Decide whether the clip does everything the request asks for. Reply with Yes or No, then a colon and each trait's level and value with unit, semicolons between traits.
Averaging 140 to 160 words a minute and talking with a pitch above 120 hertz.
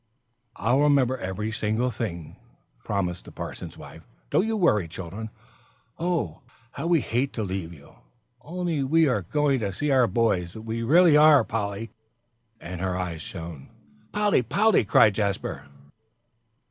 No: average, 145 wpm; low, 115 Hz